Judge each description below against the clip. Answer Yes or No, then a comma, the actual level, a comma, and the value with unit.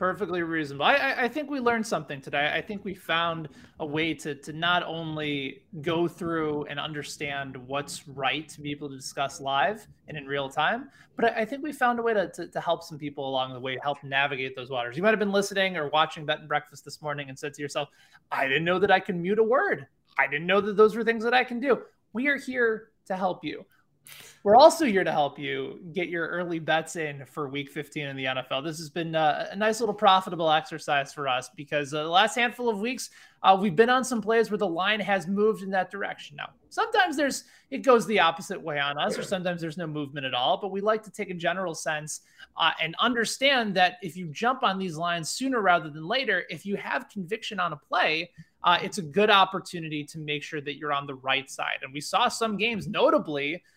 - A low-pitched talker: No, medium, 170 Hz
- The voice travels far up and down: Yes, wide, 6.1 semitones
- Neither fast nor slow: No, fast, 240 wpm